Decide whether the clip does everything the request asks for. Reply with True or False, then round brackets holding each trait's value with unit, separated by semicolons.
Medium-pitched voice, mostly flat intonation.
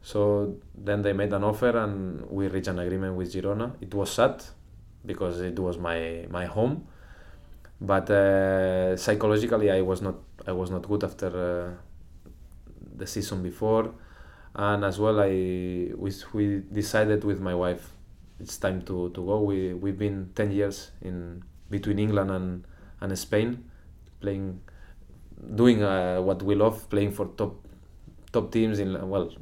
False (95 Hz; 2.3 semitones)